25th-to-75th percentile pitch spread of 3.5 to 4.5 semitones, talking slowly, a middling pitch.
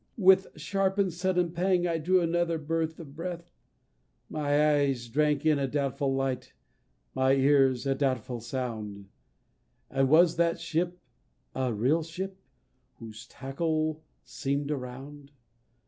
Yes: average, 4.0 semitones; slow, 130 wpm; medium, 150 Hz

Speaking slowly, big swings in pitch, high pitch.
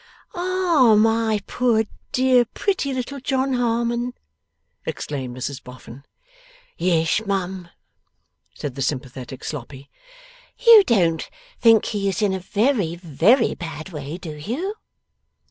Yes: slow, 115 wpm; wide, 8.1 semitones; high, 205 Hz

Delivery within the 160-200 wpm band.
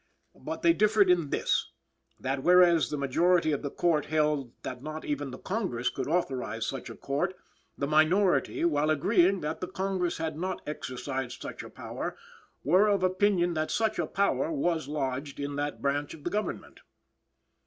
Yes: average, 175 wpm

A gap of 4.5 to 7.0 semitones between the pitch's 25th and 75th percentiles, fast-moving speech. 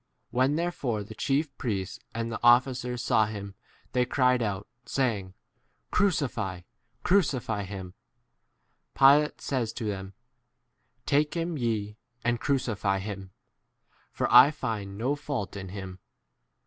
No: average, 5.0 semitones; slow, 135 wpm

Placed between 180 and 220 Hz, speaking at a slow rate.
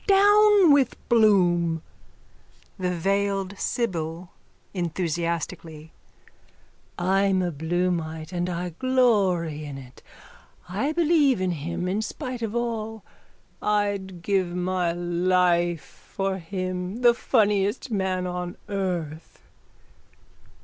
Yes: medium, 185 Hz; slow, 100 wpm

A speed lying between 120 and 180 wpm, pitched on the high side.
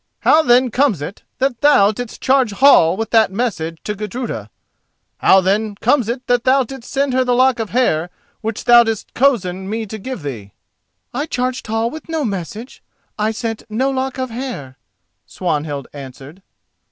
Yes: average, 175 wpm; high, 225 Hz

